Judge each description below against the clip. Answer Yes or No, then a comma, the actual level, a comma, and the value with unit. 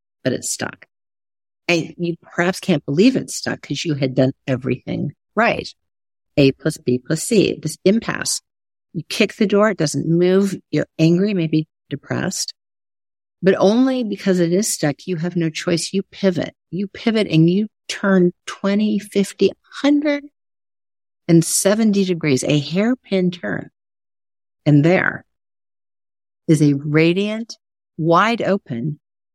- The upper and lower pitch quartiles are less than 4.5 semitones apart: No, wide, 5.6 semitones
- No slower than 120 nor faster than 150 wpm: Yes, slow, 135 wpm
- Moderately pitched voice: Yes, medium, 170 Hz